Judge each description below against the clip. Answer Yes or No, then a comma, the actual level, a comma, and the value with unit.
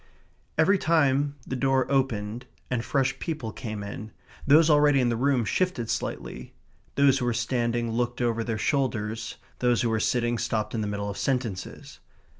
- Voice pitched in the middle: No, low, 120 Hz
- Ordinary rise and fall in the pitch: Yes, average, 3.4 semitones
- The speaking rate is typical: Yes, average, 170 wpm